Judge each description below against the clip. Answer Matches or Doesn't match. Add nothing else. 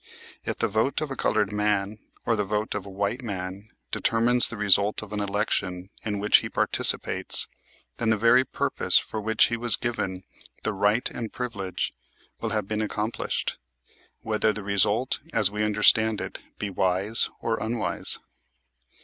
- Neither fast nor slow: Matches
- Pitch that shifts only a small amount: Matches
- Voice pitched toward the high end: Doesn't match